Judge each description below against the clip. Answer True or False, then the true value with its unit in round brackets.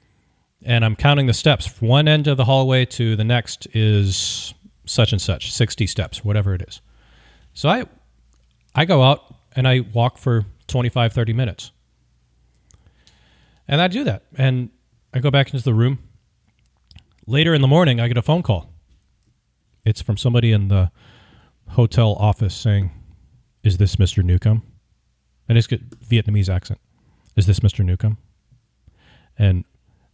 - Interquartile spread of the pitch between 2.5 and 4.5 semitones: True (3.9 semitones)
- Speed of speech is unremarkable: True (155 wpm)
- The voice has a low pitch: True (110 Hz)